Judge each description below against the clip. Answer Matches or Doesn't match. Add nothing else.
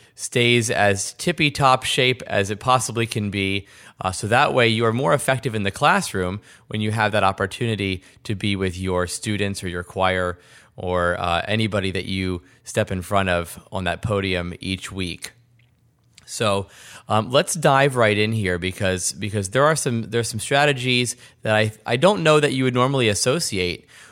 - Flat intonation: Doesn't match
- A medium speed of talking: Matches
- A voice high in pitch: Doesn't match